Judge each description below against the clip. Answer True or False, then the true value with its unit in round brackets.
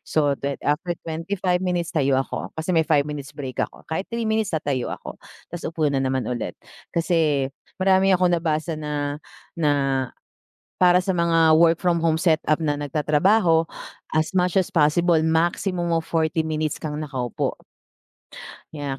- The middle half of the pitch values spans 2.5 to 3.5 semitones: True (2.9 semitones)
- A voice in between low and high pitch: True (160 Hz)